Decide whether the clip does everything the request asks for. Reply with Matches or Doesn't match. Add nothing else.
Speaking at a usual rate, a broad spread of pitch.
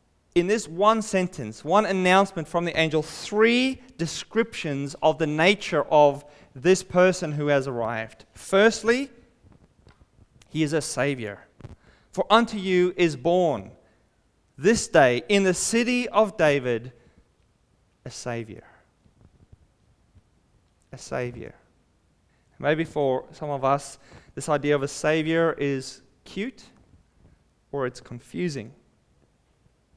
Doesn't match